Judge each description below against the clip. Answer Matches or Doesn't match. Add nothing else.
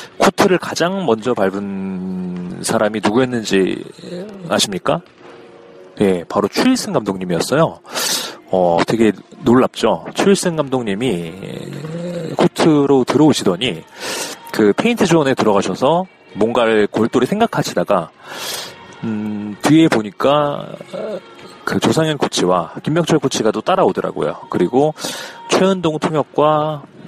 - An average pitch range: Doesn't match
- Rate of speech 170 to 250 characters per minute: Doesn't match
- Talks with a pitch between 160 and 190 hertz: Doesn't match